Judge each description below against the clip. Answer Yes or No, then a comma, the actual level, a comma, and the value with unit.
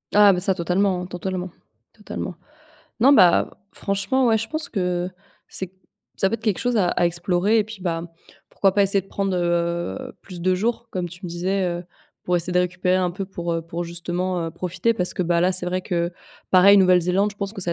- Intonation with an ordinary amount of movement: No, narrow, 2.1 semitones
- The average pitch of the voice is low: No, medium, 185 Hz